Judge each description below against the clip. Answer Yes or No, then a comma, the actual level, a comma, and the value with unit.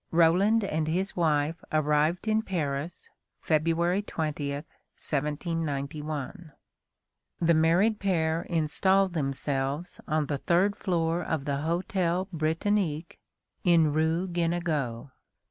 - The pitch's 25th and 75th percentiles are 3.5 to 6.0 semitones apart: No, average, 2.8 semitones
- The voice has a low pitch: No, medium, 165 Hz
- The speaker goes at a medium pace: No, slow, 100 wpm